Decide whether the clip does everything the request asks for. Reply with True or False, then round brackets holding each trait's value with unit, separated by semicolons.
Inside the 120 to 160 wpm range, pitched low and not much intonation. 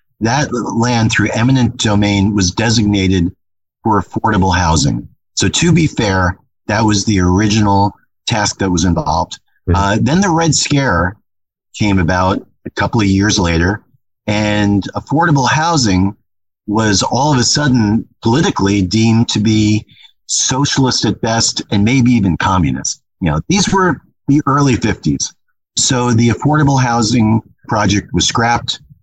False (140 wpm; 110 Hz; 4.0 semitones)